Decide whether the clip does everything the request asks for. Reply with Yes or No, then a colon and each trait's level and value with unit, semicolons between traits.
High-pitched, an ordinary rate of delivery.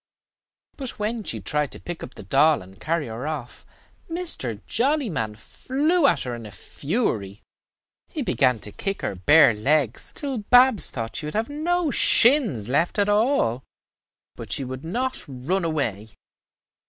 No: medium, 155 Hz; average, 160 wpm